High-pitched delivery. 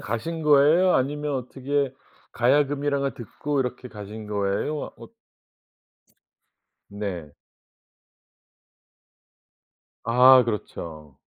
No: low, 130 Hz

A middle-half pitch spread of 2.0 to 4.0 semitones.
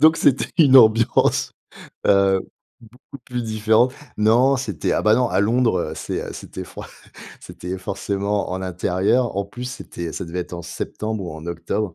No: average, 4.8 semitones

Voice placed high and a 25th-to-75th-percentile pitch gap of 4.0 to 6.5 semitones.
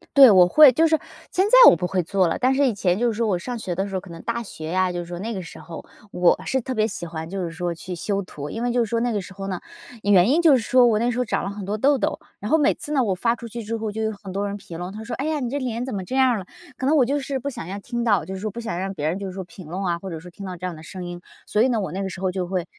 Yes: high, 200 Hz; average, 5.0 semitones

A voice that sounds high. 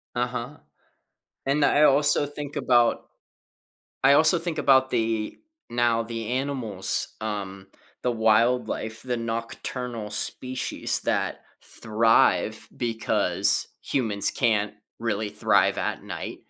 No: low, 115 Hz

